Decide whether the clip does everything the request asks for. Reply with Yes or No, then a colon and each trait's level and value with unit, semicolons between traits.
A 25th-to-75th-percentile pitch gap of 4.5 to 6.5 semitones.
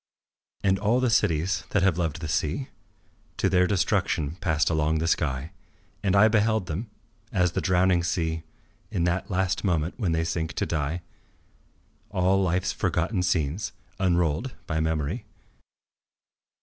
No: average, 3.3 semitones